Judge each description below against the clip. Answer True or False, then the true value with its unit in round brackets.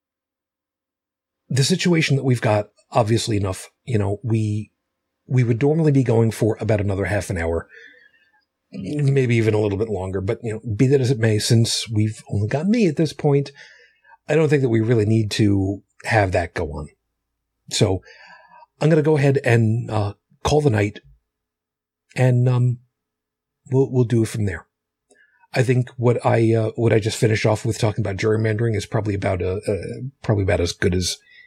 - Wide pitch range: False (4.4 semitones)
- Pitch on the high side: False (115 Hz)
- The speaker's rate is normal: True (185 wpm)